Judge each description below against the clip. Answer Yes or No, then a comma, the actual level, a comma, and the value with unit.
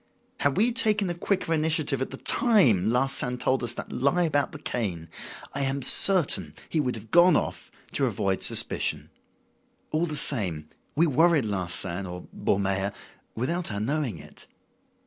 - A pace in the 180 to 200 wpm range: No, average, 160 wpm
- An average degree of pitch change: No, wide, 7.6 semitones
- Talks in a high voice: No, low, 135 Hz